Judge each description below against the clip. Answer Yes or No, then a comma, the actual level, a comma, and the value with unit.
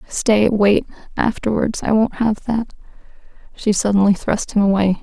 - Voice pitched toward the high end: Yes, high, 210 Hz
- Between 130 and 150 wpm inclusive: Yes, average, 145 wpm